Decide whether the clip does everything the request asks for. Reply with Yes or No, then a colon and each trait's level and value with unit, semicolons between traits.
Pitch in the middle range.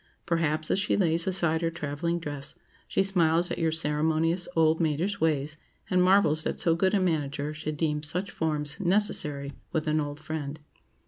Yes: medium, 160 Hz